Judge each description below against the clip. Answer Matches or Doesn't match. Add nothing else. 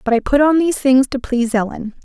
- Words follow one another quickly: Matches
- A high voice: Matches